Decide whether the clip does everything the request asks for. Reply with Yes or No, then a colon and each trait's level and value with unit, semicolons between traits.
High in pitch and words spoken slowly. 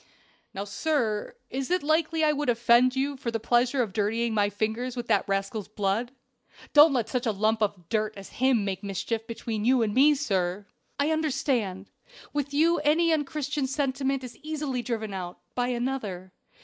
No: high, 240 Hz; average, 175 wpm